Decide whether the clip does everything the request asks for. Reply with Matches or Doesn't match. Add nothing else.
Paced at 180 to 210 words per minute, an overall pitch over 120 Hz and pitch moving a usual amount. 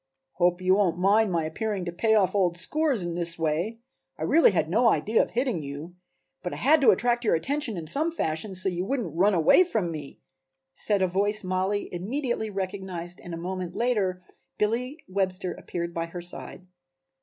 Matches